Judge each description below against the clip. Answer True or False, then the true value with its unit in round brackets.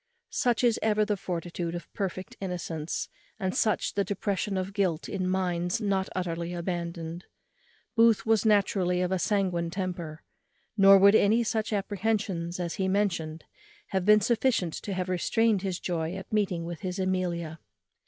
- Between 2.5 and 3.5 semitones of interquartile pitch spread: True (2.8 semitones)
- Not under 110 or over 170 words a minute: True (155 wpm)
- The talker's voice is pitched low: False (185 Hz)